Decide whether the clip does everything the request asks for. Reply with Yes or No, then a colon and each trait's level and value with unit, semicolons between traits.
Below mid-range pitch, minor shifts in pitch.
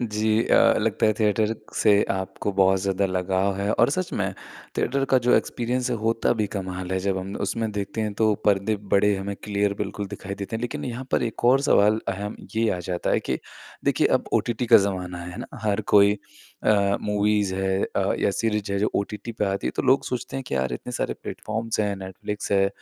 Yes: low, 105 Hz; narrow, 2.3 semitones